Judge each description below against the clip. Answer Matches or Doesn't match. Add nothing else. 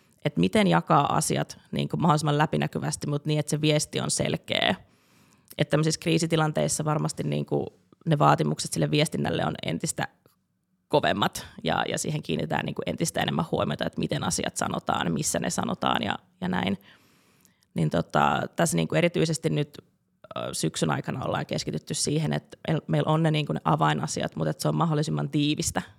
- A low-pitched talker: Doesn't match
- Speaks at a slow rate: Doesn't match